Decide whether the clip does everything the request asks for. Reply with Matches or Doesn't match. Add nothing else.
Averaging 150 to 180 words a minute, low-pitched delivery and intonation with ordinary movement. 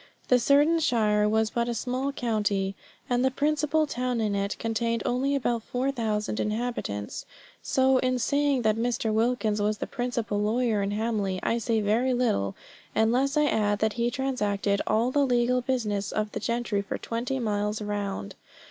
Doesn't match